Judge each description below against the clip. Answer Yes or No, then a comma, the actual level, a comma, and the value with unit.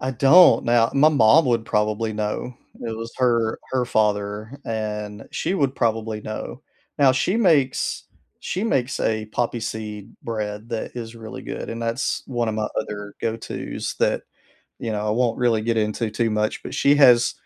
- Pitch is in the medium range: No, low, 115 Hz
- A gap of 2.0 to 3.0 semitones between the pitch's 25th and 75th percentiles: Yes, narrow, 2.6 semitones